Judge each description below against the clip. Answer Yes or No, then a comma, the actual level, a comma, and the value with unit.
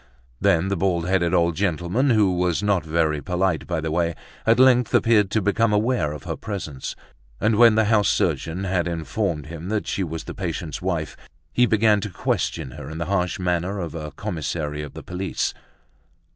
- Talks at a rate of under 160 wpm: No, average, 190 wpm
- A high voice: No, very low, 90 Hz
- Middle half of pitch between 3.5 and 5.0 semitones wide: Yes, average, 4.1 semitones